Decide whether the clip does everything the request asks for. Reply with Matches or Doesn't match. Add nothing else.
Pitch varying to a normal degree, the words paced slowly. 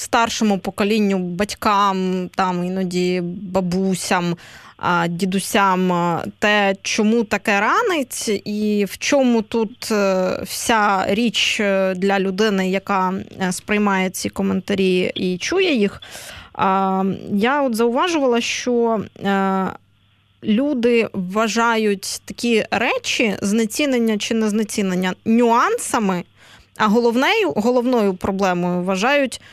Matches